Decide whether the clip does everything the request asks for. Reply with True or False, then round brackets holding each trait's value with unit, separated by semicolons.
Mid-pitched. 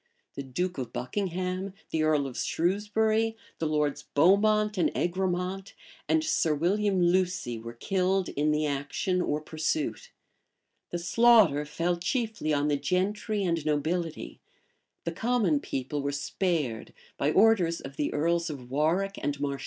True (170 Hz)